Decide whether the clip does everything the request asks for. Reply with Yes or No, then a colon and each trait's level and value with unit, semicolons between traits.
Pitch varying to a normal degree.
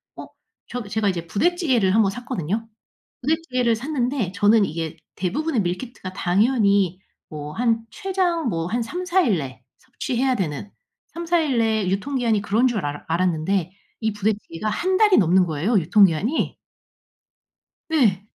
No: wide, 5.8 semitones